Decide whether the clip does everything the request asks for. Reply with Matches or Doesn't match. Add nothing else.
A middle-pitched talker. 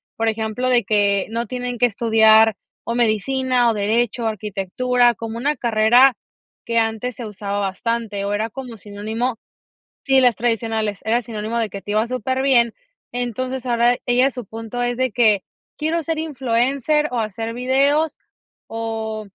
Doesn't match